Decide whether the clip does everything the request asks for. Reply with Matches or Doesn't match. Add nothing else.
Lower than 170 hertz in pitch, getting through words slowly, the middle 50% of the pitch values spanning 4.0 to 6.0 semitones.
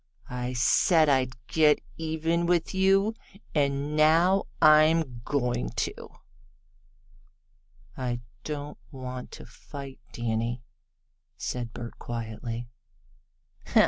Matches